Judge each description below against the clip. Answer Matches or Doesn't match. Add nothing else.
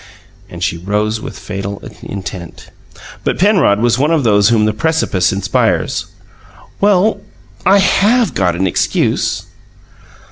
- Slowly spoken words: Matches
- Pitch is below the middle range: Matches